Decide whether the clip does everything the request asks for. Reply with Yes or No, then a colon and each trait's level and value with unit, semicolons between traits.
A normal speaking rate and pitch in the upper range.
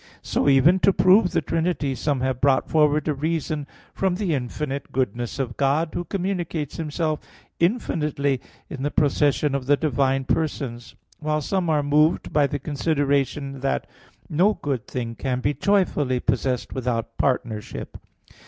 No: average, 150 wpm; medium, 145 Hz